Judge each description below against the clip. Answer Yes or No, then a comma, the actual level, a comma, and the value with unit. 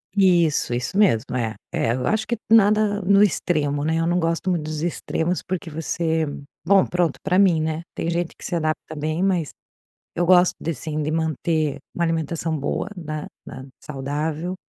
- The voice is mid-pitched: Yes, medium, 165 Hz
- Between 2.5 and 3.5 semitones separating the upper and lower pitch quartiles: Yes, average, 2.8 semitones